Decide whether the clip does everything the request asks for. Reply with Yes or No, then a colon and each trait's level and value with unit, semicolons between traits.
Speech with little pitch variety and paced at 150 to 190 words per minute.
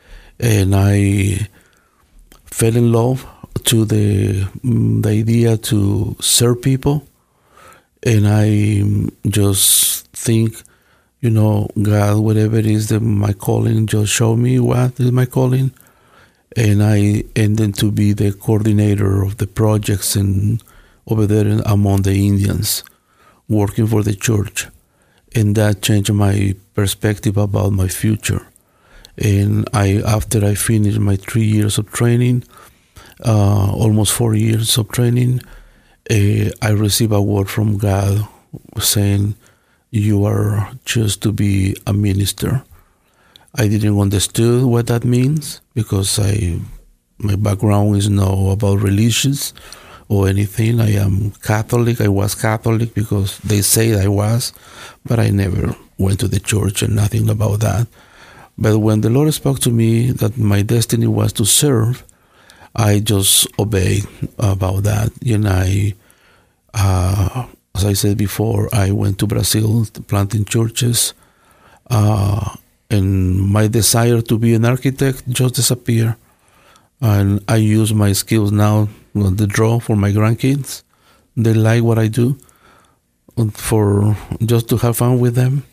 No: narrow, 2.3 semitones; slow, 135 wpm